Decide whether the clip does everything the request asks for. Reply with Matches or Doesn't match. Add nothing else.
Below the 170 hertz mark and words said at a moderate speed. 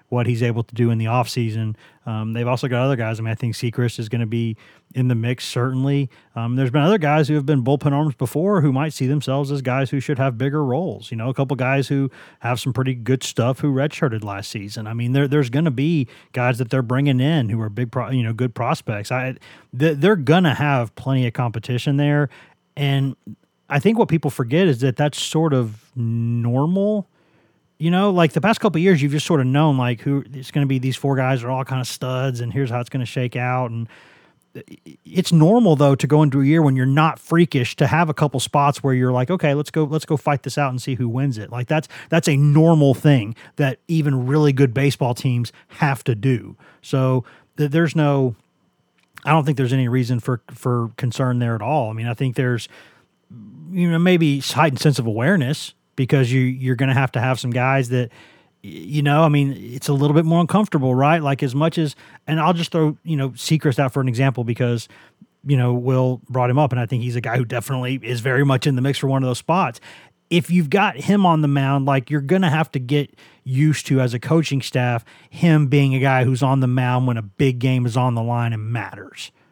Doesn't match